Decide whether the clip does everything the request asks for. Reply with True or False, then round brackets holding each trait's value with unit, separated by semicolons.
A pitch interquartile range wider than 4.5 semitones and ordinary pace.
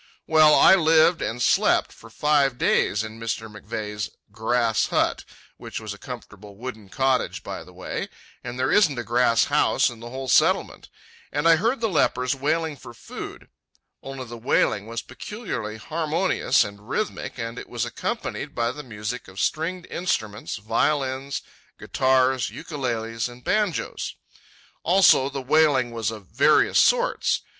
True (5.2 semitones; 150 wpm)